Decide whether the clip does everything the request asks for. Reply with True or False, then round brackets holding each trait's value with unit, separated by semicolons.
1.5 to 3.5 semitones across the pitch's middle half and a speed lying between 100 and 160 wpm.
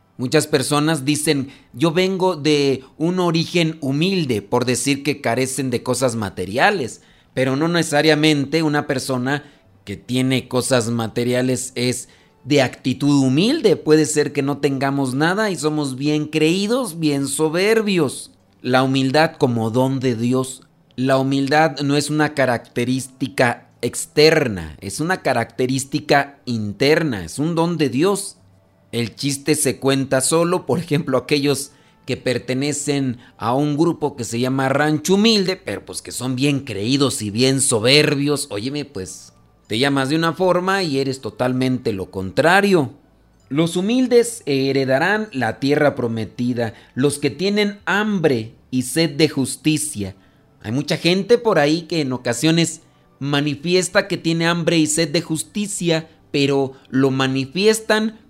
False (3.9 semitones; 140 wpm)